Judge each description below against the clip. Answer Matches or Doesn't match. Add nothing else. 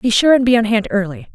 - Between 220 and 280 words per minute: Doesn't match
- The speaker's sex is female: Matches